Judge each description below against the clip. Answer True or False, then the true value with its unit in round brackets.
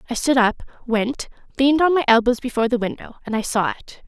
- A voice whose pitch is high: True (245 Hz)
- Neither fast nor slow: False (220 wpm)